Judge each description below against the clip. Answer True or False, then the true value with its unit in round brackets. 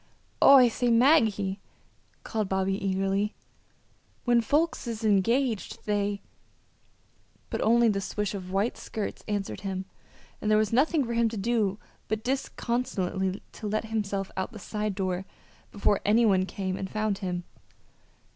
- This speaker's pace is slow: False (150 wpm)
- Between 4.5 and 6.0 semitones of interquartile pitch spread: False (3.1 semitones)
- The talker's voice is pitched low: False (210 Hz)